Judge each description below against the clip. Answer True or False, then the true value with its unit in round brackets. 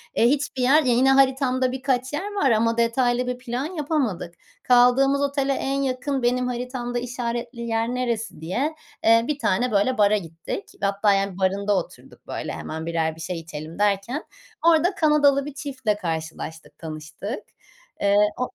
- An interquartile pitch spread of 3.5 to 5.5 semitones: True (5.1 semitones)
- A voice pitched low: False (245 Hz)